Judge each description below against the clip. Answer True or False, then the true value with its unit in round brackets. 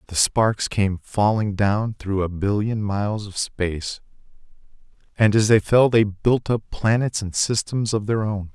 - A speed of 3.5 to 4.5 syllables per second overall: True (4.2 syllables/s)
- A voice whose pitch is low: True (105 Hz)